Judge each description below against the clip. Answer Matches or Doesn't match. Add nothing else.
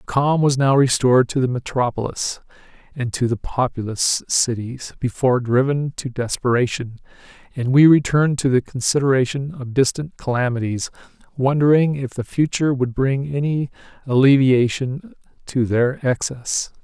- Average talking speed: Doesn't match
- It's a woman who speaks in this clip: Doesn't match